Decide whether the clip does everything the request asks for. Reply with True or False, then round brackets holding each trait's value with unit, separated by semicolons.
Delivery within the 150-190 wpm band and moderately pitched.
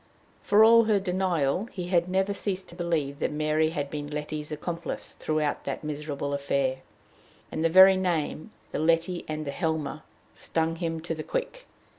True (170 wpm; 165 Hz)